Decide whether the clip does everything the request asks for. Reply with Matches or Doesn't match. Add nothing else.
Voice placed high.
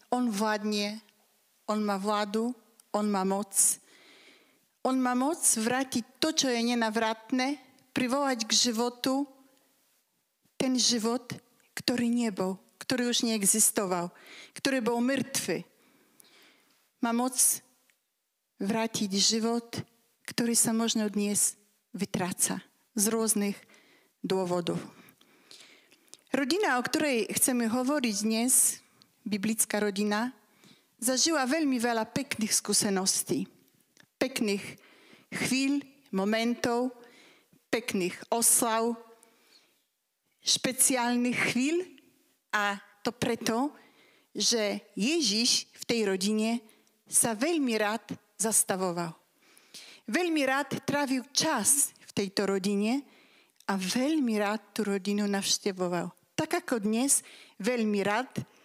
Matches